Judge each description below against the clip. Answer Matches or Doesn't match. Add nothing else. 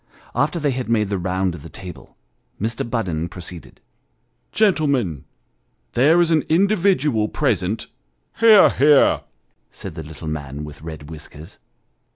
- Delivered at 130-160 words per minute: Matches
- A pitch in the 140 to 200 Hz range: Doesn't match